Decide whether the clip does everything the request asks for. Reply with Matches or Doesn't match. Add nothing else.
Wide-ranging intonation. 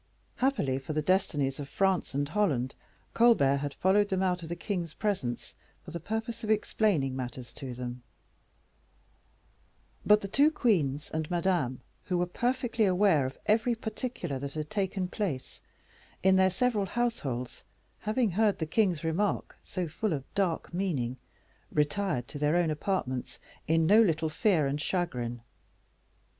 Matches